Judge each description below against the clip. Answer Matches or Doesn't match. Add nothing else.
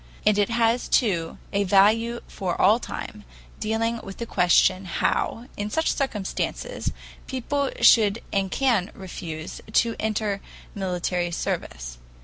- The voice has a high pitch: Matches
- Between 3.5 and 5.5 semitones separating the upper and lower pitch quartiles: Matches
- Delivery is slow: Matches